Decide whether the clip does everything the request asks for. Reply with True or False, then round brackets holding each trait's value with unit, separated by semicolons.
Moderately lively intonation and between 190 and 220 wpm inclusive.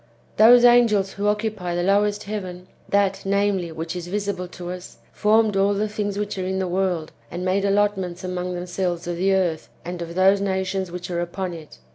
False (2.3 semitones; 195 wpm)